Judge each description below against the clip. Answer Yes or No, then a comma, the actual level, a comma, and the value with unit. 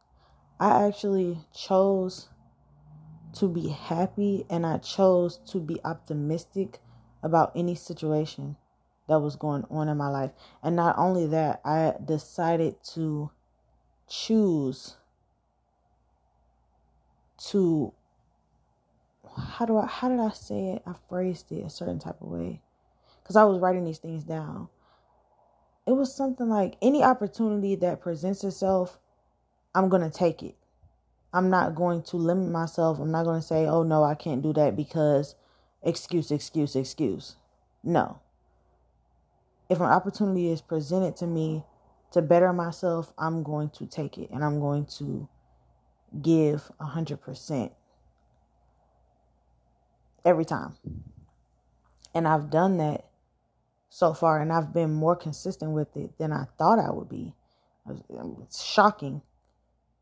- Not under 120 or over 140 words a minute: Yes, slow, 135 wpm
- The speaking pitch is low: No, medium, 160 Hz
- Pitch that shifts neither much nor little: Yes, average, 3.7 semitones